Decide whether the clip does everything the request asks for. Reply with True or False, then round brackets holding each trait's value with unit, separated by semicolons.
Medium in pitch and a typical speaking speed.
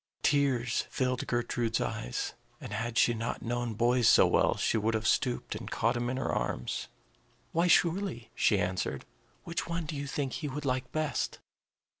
False (120 Hz; 175 wpm)